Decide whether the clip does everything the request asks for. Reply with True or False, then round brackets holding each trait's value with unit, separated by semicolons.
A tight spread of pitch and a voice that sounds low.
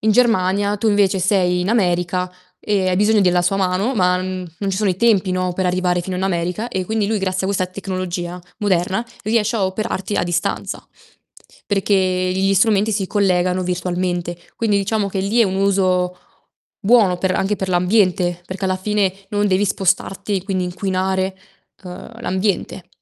False (2.0 semitones; 190 Hz)